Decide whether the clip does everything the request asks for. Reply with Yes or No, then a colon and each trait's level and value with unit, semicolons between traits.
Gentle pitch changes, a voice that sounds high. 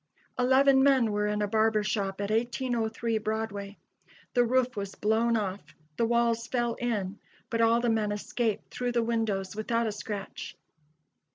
Yes: narrow, 2.3 semitones; high, 225 Hz